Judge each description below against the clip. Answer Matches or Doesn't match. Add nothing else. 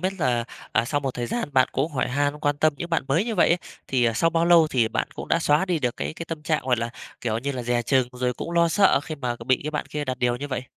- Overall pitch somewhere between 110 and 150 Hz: Matches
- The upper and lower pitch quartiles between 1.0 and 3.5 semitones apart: Doesn't match